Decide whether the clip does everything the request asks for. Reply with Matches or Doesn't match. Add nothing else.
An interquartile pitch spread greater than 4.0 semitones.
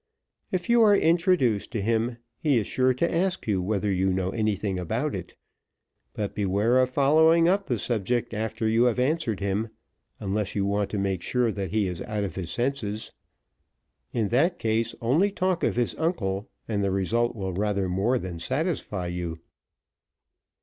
Matches